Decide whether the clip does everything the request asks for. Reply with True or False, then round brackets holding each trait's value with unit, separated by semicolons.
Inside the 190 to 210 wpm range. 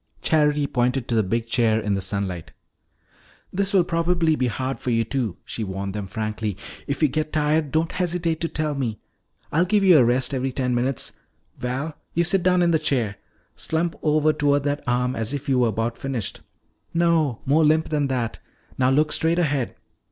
True (195 wpm)